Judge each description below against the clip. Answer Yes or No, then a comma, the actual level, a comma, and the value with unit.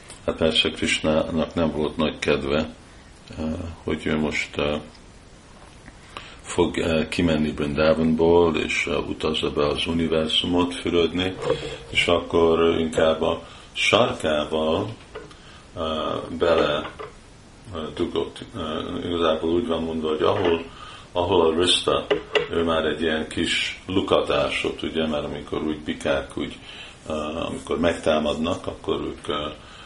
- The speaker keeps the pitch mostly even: Yes, narrow, 1.7 semitones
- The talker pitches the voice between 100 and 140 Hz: No, very low, 80 Hz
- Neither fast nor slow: No, slow, 100 wpm